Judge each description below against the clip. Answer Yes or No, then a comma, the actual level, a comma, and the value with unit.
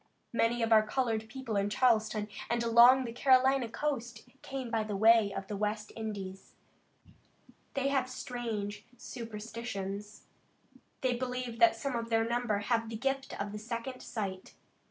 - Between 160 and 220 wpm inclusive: No, average, 150 wpm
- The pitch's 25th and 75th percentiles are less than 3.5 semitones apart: Yes, average, 2.9 semitones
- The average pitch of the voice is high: Yes, high, 230 Hz